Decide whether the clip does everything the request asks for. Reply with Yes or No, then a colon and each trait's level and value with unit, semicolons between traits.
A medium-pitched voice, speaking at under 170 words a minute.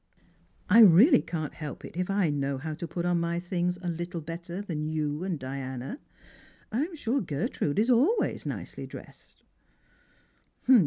Yes: medium, 170 Hz; average, 155 wpm